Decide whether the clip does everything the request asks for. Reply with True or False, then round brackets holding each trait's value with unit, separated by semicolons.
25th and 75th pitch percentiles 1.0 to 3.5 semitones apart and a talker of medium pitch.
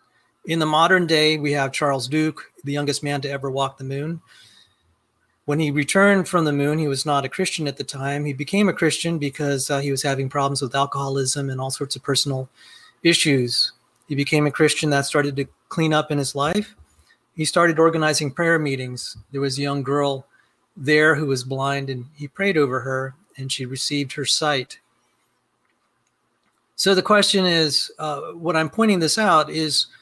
True (2.5 semitones; 145 Hz)